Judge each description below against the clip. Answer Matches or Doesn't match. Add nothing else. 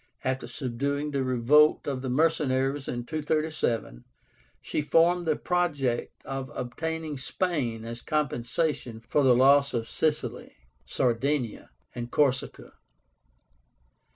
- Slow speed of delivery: Matches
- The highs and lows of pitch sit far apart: Doesn't match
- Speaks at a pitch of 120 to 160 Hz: Matches